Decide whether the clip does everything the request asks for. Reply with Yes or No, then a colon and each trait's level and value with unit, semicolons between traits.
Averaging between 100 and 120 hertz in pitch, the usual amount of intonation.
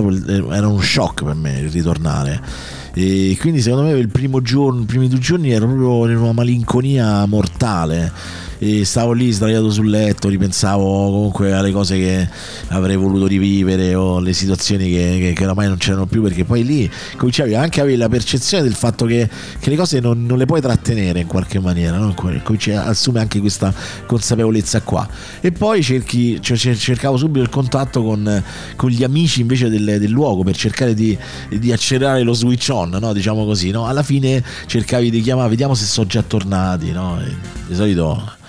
Yes: low, 110 Hz; average, 4.5 semitones